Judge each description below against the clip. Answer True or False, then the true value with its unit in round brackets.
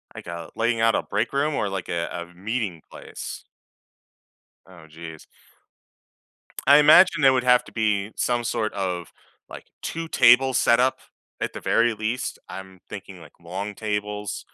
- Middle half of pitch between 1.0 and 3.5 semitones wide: False (4.9 semitones)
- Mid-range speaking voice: False (105 Hz)